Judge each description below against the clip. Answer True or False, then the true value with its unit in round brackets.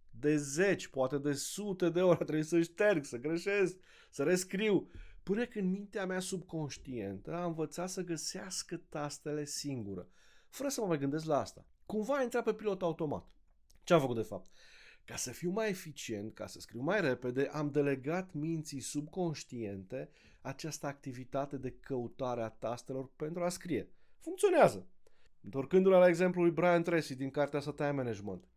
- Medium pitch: True (155 Hz)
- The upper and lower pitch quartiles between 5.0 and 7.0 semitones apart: True (5.3 semitones)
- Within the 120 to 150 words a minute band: False (165 wpm)